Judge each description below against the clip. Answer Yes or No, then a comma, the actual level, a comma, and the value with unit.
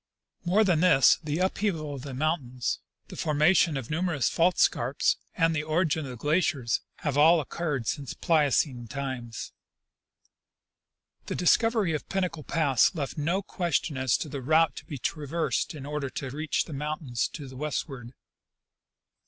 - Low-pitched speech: No, medium, 150 Hz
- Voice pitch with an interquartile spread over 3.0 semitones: Yes, average, 3.6 semitones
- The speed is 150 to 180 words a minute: Yes, average, 155 wpm